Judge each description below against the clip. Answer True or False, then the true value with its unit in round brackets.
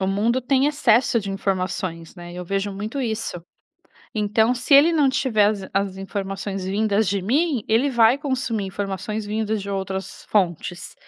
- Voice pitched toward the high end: True (210 Hz)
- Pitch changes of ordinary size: True (3.7 semitones)